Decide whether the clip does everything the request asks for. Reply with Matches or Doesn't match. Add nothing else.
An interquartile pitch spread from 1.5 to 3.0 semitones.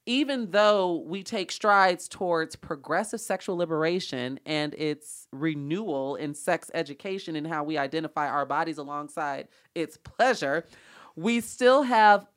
Doesn't match